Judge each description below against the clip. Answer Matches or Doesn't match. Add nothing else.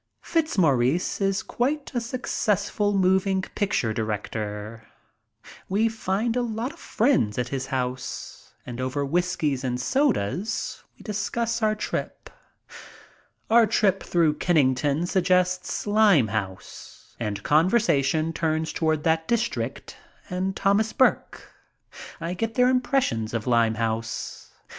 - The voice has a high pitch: Doesn't match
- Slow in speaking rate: Matches